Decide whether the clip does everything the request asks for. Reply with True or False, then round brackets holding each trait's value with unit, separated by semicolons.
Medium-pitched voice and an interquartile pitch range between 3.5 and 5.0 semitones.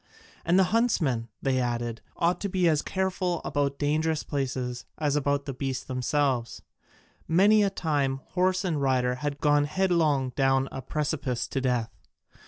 True (145 Hz; 4.4 semitones)